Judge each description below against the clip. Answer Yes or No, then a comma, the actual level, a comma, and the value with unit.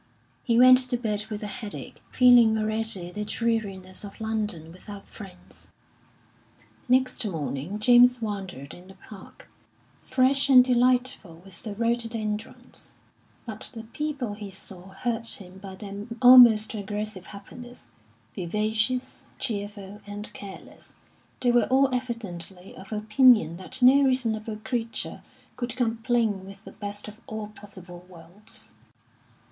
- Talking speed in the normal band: No, slow, 130 wpm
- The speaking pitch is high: Yes, high, 215 Hz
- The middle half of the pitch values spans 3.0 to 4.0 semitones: Yes, average, 3.6 semitones